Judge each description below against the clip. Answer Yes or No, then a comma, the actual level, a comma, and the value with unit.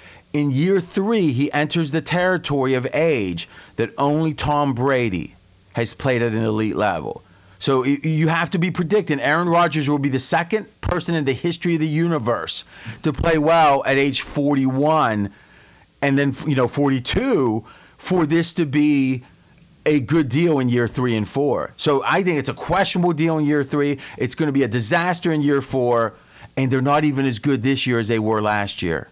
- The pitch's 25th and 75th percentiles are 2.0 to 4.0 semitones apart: No, average, 4.8 semitones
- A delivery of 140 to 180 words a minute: No, average, 190 wpm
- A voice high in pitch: No, medium, 140 Hz